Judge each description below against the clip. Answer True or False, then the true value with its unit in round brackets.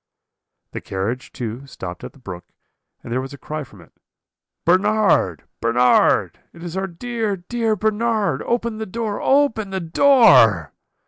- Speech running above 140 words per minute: True (150 wpm)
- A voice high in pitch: False (175 Hz)